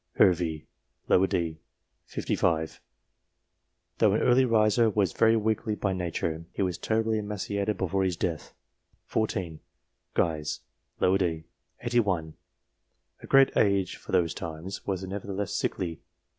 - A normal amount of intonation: Yes, average, 4.3 semitones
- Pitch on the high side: No, very low, 95 Hz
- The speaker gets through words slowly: Yes, slow, 125 wpm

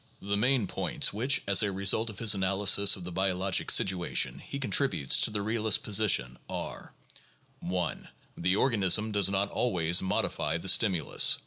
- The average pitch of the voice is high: No, low, 100 Hz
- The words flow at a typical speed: Yes, average, 155 wpm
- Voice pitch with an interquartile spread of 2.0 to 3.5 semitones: Yes, average, 2.9 semitones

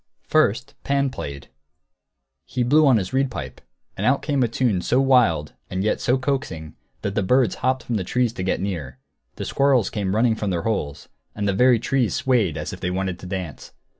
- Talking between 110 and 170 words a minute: No, fast, 205 wpm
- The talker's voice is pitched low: Yes, low, 110 Hz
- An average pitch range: No, wide, 5.8 semitones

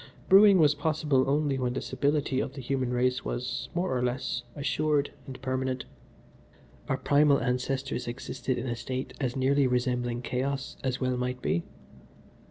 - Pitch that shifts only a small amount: Yes, narrow, 2.0 semitones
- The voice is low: Yes, low, 130 Hz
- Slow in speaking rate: No, average, 160 wpm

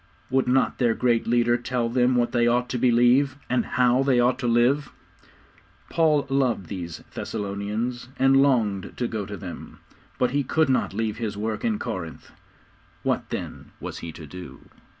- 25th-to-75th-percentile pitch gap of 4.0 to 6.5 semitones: No, average, 2.9 semitones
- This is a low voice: Yes, low, 120 Hz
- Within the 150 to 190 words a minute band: Yes, average, 170 wpm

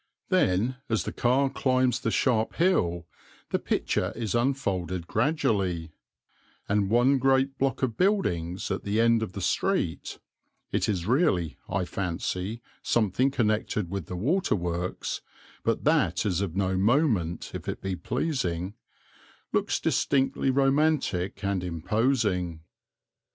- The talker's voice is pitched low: Yes, low, 105 Hz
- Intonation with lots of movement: Yes, wide, 6.4 semitones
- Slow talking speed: Yes, slow, 130 wpm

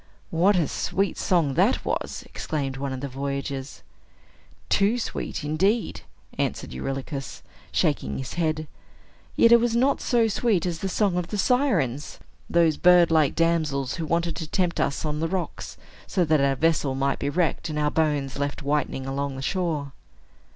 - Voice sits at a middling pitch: Yes, medium, 155 Hz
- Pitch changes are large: No, average, 4.3 semitones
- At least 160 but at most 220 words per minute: Yes, average, 170 wpm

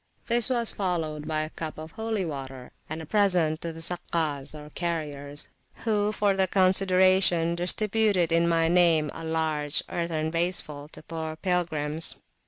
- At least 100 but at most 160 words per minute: Yes, average, 155 wpm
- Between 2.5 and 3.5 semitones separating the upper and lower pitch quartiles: Yes, average, 3.2 semitones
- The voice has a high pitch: No, medium, 165 Hz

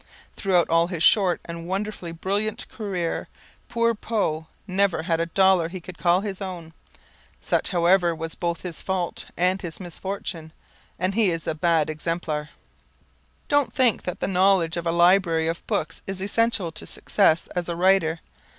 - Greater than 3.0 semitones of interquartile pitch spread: No, narrow, 2.6 semitones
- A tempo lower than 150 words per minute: No, average, 165 wpm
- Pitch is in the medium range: Yes, medium, 180 Hz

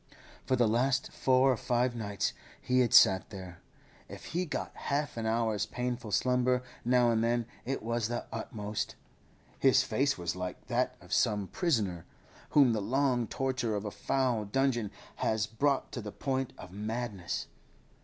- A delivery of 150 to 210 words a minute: Yes, average, 165 wpm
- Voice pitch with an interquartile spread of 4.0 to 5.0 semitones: No, average, 3.4 semitones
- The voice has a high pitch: No, low, 120 Hz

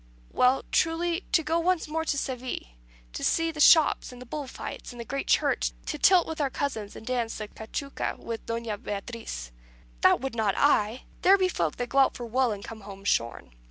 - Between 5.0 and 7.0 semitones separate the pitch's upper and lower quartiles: Yes, wide, 5.6 semitones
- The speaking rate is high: Yes, fast, 210 wpm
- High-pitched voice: Yes, very high, 255 Hz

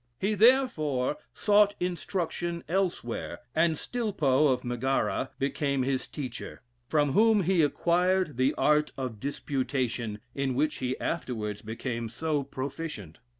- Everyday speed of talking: No, slow, 120 wpm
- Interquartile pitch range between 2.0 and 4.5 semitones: No, average, 5.1 semitones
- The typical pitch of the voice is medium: Yes, medium, 145 Hz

